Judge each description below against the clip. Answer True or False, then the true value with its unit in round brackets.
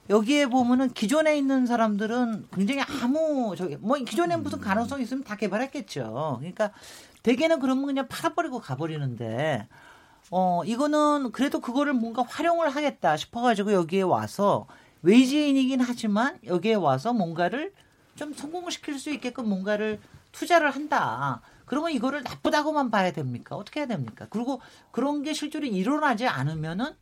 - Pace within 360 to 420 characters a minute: True (365 characters per minute)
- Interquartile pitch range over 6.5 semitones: False (5.9 semitones)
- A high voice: True (250 Hz)